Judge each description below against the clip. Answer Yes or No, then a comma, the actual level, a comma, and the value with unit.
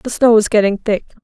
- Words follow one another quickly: Yes, fast, 245 wpm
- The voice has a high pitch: Yes, high, 215 Hz